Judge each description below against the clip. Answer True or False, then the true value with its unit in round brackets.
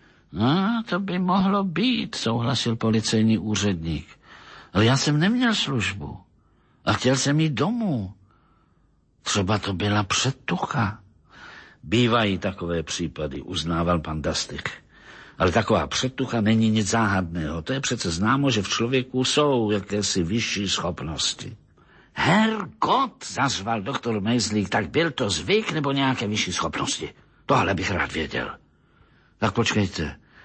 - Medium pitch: False (115 Hz)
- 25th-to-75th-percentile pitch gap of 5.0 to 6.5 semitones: True (5.6 semitones)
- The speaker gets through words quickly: False (125 wpm)